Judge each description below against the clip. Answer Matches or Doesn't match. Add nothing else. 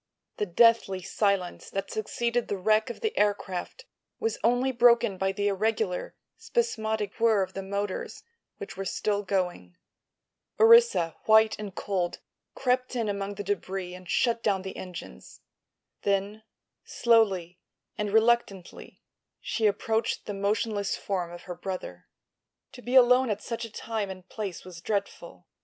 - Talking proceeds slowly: Doesn't match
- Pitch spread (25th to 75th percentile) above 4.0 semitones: Doesn't match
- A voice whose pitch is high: Matches